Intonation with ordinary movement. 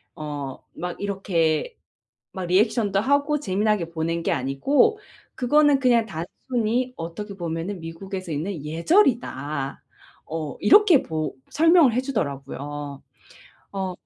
No: wide, 7.5 semitones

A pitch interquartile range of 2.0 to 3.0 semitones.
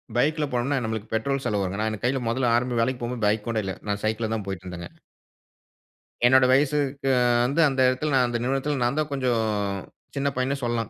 No: average, 3.5 semitones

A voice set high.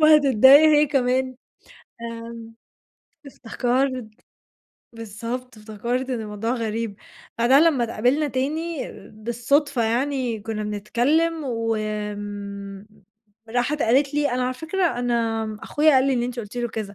Yes: high, 240 Hz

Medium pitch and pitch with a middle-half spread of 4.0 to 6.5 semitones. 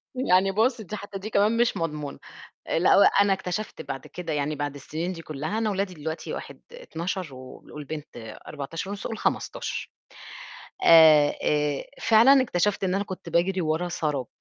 Yes: medium, 175 Hz; average, 5.1 semitones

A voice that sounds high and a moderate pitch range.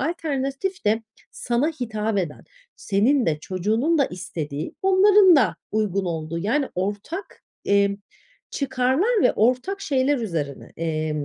No: high, 225 Hz; wide, 8.0 semitones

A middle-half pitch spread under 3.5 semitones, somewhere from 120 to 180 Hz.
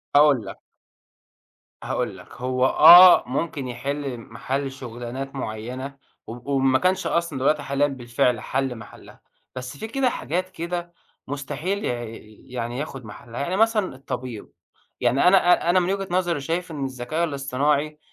No: average, 5.1 semitones; medium, 140 Hz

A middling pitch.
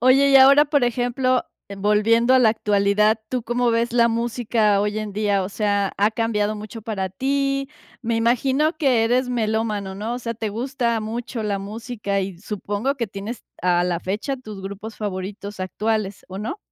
No: high, 220 Hz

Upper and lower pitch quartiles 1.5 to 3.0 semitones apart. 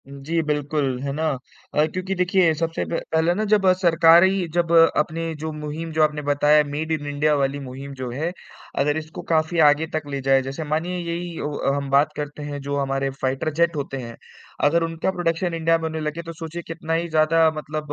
Yes: narrow, 2.4 semitones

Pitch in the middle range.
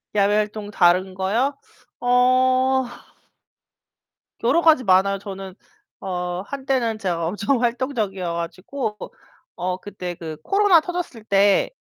No: high, 210 Hz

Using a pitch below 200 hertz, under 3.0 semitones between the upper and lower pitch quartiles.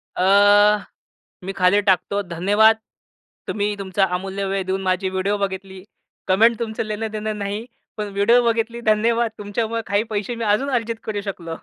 No: high, 205 Hz; narrow, 2.4 semitones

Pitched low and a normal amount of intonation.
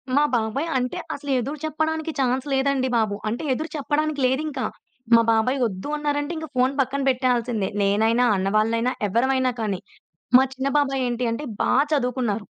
No: very high, 255 Hz; average, 3.9 semitones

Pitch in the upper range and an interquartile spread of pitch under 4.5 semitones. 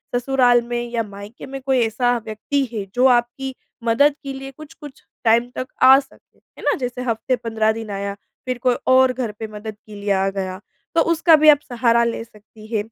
Yes: high, 240 Hz; average, 3.3 semitones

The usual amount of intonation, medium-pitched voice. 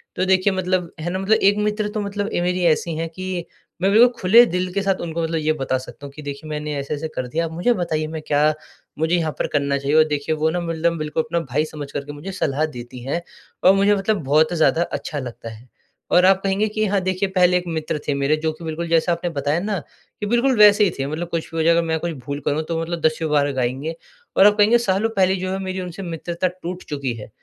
Yes: average, 3.7 semitones; medium, 165 Hz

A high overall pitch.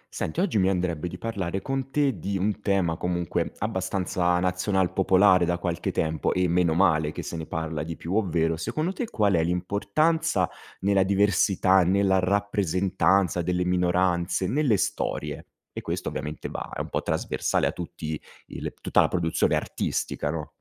No: very low, 90 Hz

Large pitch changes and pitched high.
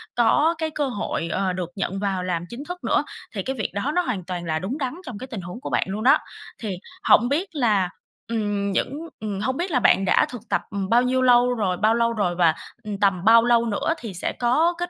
No: average, 4.9 semitones; high, 225 Hz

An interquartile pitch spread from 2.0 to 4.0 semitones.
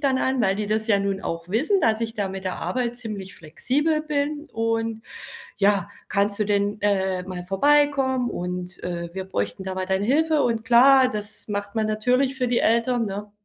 No: average, 4.8 semitones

